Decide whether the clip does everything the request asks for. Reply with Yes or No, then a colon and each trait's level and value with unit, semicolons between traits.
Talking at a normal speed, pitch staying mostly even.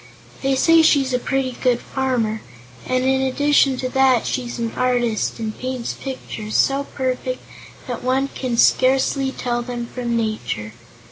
Yes: average, 150 wpm; narrow, 1.9 semitones